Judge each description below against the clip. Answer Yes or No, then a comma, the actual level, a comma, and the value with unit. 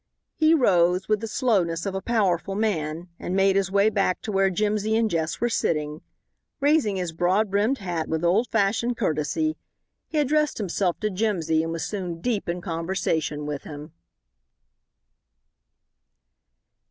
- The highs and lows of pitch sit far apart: No, average, 4.5 semitones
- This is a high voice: Yes, high, 195 Hz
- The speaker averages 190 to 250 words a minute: No, average, 155 wpm